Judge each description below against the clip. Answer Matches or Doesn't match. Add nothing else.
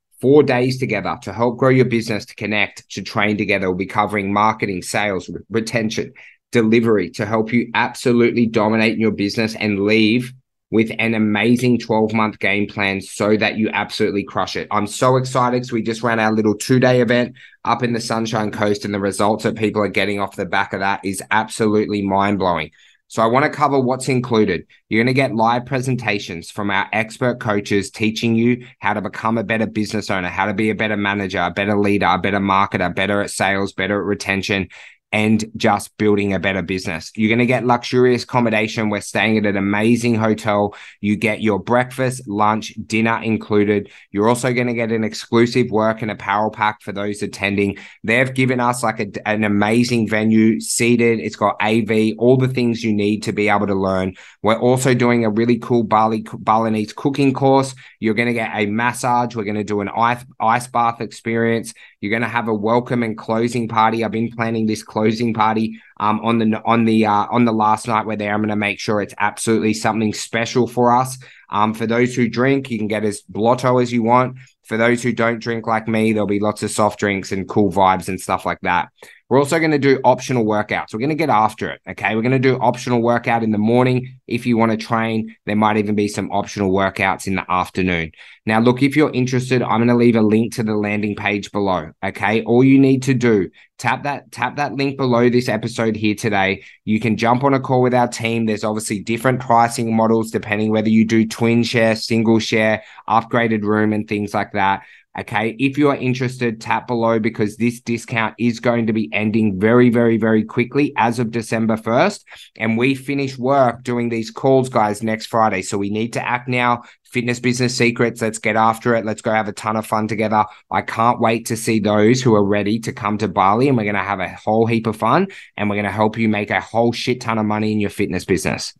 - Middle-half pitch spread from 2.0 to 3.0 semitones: Matches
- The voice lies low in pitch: Matches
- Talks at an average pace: Doesn't match